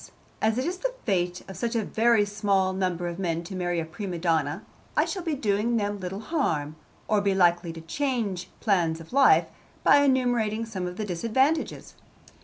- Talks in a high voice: Yes, high, 200 Hz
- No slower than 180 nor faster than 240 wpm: Yes, average, 185 wpm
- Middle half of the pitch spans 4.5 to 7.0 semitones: Yes, average, 5.0 semitones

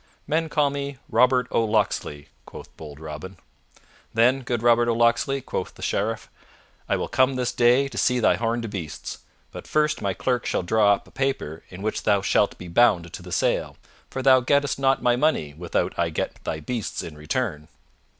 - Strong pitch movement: Yes, wide, 5.9 semitones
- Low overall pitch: Yes, low, 115 Hz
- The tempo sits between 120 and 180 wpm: No, average, 190 wpm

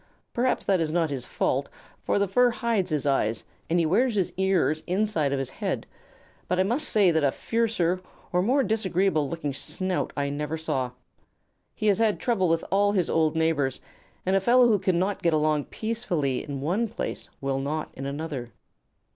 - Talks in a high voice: No, medium, 175 Hz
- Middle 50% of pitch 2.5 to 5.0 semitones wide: No, wide, 5.4 semitones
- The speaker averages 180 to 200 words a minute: Yes, average, 190 wpm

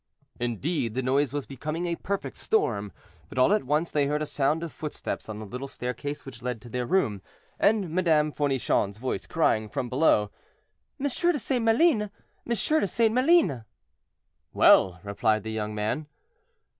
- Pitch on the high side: No, medium, 145 Hz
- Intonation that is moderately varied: No, wide, 7.7 semitones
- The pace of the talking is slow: No, average, 170 wpm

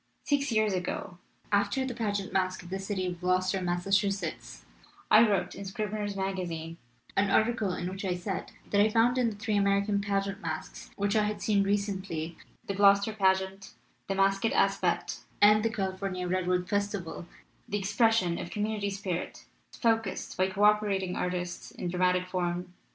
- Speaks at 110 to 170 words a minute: Yes, average, 165 wpm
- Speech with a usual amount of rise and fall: No, narrow, 2.2 semitones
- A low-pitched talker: No, high, 195 Hz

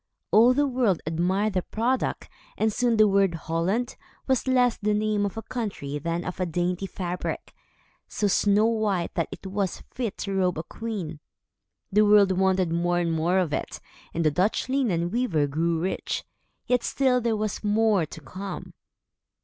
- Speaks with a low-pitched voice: No, high, 195 Hz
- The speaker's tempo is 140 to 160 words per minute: No, average, 175 wpm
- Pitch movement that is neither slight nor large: Yes, average, 4.2 semitones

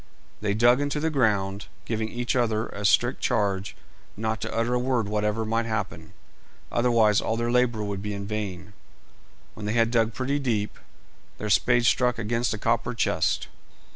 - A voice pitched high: No, low, 110 Hz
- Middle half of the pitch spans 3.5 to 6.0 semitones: No, narrow, 2.5 semitones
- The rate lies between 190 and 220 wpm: No, average, 170 wpm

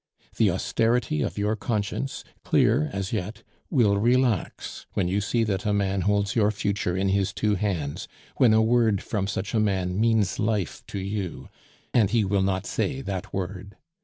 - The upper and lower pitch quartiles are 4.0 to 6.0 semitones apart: No, narrow, 2.5 semitones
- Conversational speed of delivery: Yes, average, 175 wpm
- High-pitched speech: No, low, 100 Hz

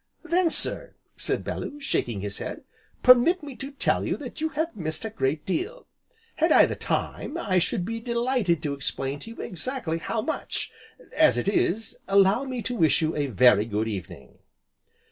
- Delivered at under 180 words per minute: No, average, 185 wpm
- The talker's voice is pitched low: No, high, 200 Hz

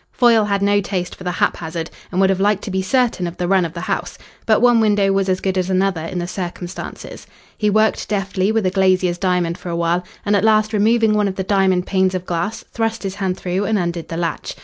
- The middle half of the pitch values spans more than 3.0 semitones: No, narrow, 2.4 semitones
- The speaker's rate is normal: No, fast, 245 wpm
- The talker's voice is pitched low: No, high, 190 Hz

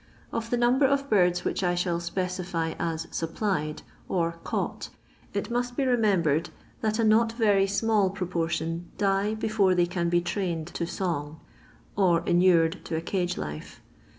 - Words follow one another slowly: No, average, 160 wpm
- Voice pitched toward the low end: No, medium, 180 Hz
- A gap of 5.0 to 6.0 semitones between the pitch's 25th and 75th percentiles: No, average, 4.1 semitones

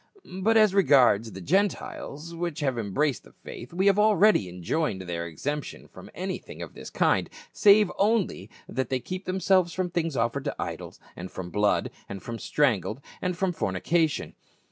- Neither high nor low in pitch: Yes, medium, 150 Hz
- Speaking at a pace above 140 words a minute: Yes, average, 170 wpm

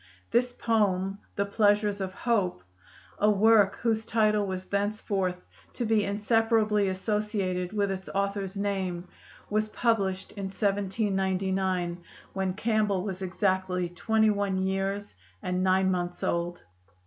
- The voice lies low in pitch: No, high, 200 Hz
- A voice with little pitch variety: Yes, narrow, 2.1 semitones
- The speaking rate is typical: No, slow, 125 wpm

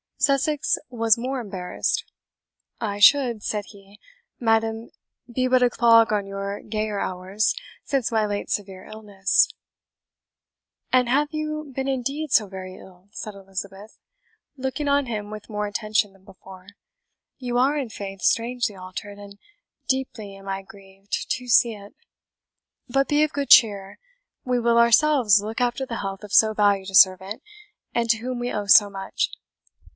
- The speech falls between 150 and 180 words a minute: Yes, average, 155 wpm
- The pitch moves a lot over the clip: No, average, 3.9 semitones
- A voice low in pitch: No, high, 215 Hz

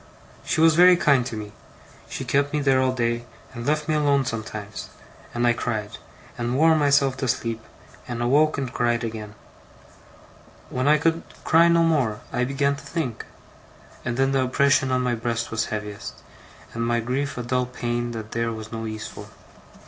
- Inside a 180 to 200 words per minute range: Yes, average, 185 wpm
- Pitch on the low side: Yes, low, 125 Hz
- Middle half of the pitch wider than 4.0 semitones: No, average, 3.5 semitones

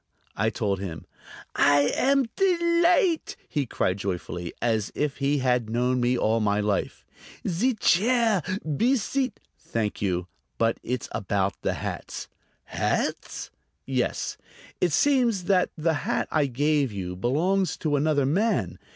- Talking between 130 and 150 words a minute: Yes, slow, 135 wpm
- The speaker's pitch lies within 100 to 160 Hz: Yes, medium, 140 Hz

